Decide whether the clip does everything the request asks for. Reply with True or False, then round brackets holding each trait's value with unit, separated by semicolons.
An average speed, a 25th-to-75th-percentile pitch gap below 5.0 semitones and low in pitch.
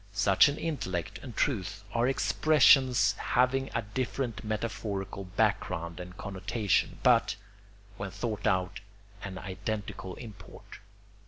False (110 wpm; 4.3 semitones; 105 Hz)